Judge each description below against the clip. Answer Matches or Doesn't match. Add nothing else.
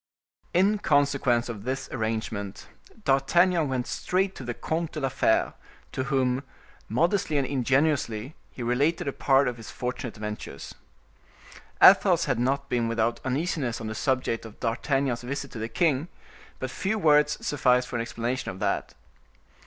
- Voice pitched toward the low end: Matches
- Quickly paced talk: Doesn't match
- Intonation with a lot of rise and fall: Doesn't match